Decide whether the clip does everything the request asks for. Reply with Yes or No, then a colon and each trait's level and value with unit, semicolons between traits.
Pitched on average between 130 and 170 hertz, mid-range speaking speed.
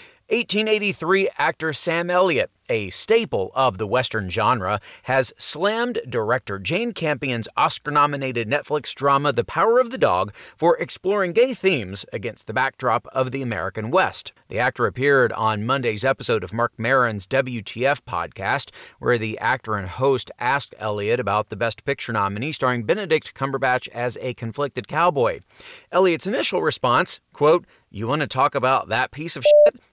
Yes: low, 135 Hz; average, 155 wpm